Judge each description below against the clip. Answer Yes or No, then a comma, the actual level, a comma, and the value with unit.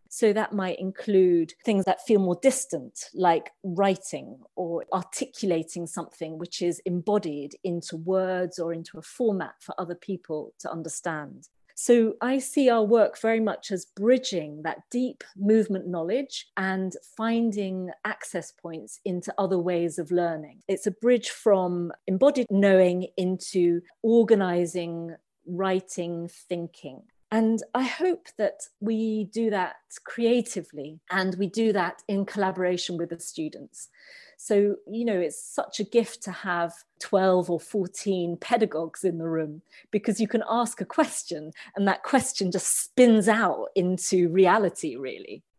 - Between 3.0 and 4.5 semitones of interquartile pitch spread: Yes, average, 4.2 semitones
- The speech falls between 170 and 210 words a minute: No, average, 140 wpm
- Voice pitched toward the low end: No, high, 190 Hz